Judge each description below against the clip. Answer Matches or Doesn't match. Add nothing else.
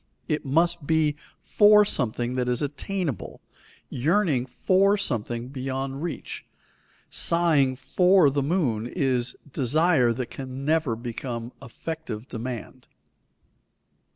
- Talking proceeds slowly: Matches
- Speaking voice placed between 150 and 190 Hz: Doesn't match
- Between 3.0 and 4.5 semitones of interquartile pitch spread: Doesn't match